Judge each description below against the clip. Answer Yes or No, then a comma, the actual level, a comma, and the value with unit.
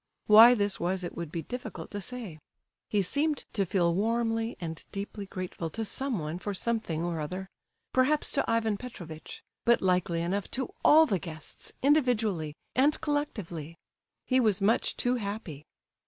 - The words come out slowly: No, average, 155 wpm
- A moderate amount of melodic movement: No, wide, 5.7 semitones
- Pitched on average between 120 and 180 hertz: No, high, 205 Hz